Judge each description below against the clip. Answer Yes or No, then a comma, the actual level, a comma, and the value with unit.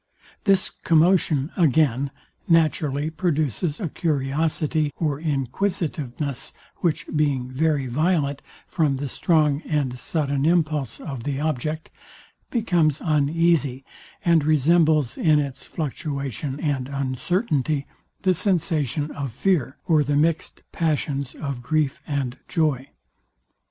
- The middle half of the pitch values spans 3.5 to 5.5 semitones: No, average, 2.8 semitones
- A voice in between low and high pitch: Yes, medium, 150 Hz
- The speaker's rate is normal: No, slow, 110 wpm